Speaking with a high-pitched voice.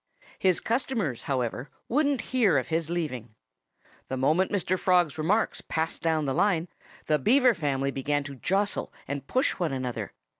No: medium, 160 Hz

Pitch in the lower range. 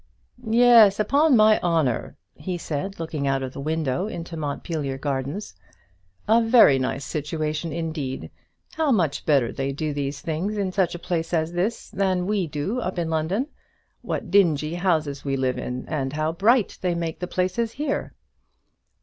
No: medium, 165 Hz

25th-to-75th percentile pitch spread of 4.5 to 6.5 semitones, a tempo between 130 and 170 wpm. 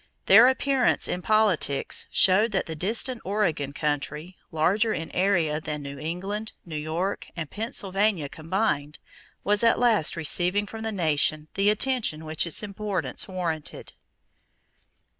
Yes: average, 5.2 semitones; slow, 135 wpm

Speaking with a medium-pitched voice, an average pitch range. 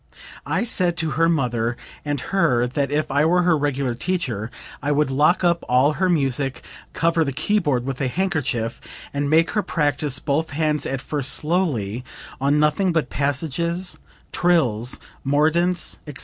Yes: medium, 145 Hz; average, 3.9 semitones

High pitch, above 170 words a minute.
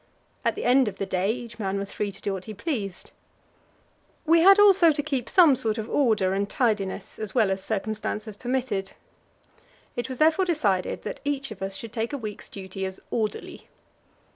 Yes: high, 220 Hz; average, 190 wpm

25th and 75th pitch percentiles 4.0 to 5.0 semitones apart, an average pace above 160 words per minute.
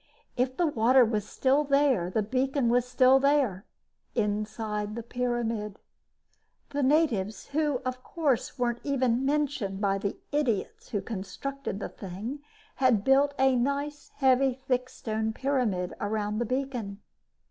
No: average, 4.4 semitones; slow, 135 wpm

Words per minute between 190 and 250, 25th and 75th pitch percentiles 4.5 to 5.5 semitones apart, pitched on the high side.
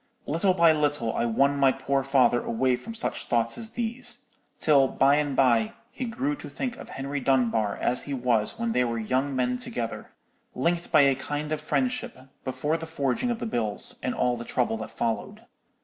No: average, 195 wpm; average, 5.0 semitones; low, 135 Hz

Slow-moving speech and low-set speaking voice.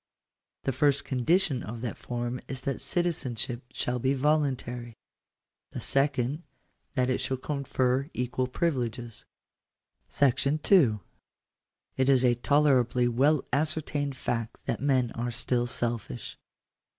Yes: slow, 120 wpm; low, 130 Hz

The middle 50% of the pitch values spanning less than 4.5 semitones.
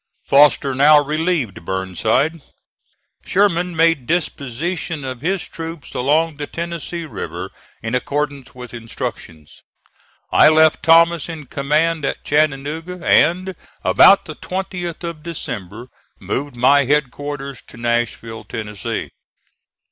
No: average, 4.8 semitones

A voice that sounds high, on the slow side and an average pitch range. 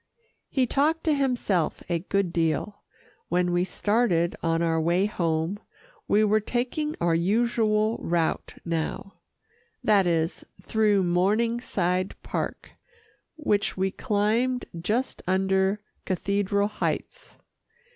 Yes: high, 200 Hz; slow, 110 wpm; average, 4.2 semitones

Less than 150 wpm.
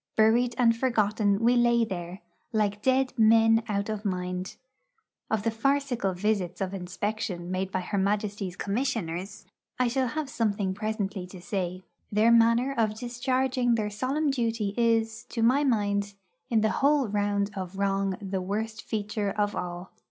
No: average, 155 wpm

